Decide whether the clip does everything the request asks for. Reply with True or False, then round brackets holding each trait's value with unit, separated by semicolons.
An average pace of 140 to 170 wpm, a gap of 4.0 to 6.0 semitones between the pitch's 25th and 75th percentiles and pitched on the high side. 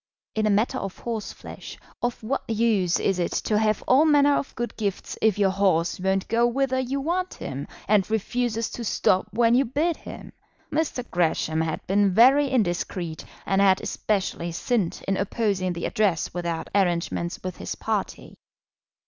True (165 wpm; 4.6 semitones; 210 Hz)